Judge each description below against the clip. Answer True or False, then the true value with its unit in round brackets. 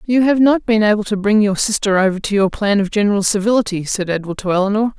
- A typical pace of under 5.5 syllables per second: False (6.4 syllables/s)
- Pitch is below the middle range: False (205 Hz)